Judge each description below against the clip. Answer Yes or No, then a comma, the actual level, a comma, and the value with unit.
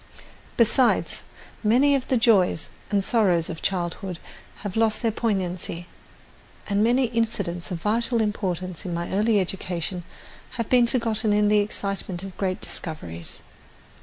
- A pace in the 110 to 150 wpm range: Yes, slow, 135 wpm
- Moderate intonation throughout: Yes, average, 4.2 semitones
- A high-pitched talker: Yes, high, 205 Hz